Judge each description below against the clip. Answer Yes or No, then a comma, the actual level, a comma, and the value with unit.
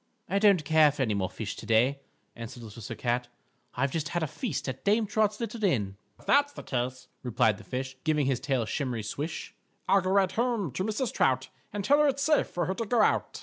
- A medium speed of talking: No, fast, 235 wpm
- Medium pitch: Yes, medium, 150 Hz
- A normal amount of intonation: No, wide, 8.9 semitones